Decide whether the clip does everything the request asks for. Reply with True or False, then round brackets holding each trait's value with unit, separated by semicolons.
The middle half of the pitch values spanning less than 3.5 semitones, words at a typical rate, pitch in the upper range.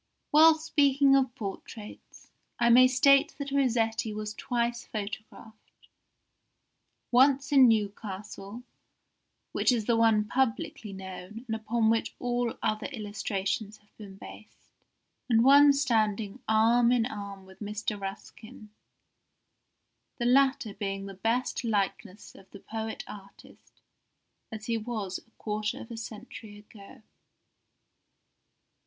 False (2.9 semitones; 120 wpm; 225 Hz)